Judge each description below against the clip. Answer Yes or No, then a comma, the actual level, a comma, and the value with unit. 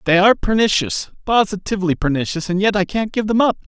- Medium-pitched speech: No, high, 195 Hz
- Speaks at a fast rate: No, average, 190 wpm